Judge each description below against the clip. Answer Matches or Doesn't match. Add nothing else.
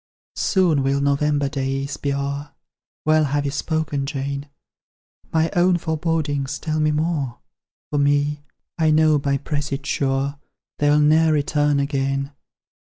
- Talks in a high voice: Doesn't match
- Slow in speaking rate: Matches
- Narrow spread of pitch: Matches